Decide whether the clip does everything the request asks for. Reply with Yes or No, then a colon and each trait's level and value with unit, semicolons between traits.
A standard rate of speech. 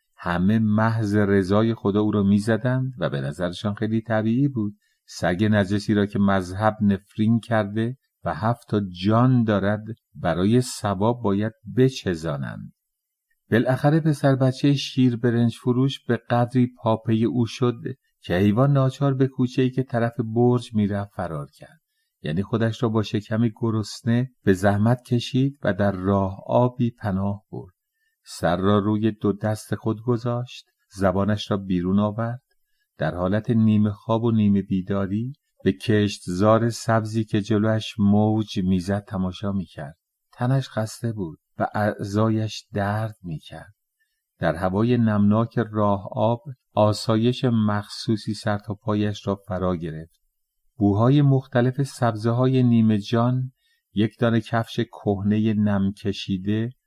Yes: average, 135 wpm